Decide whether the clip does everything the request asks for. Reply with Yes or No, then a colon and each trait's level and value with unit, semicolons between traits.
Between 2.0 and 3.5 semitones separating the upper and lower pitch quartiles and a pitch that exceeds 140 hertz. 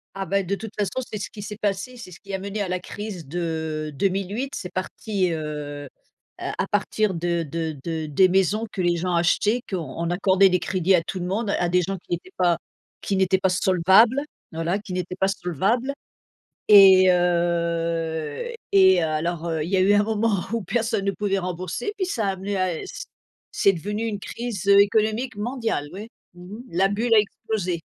Yes: average, 3.2 semitones; high, 190 Hz